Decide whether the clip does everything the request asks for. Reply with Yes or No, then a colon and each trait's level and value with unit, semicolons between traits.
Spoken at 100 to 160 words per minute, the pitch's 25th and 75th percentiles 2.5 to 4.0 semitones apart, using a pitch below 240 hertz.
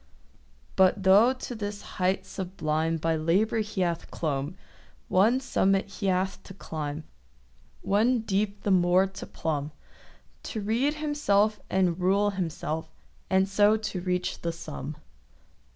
Yes: slow, 135 wpm; average, 3.6 semitones; high, 190 Hz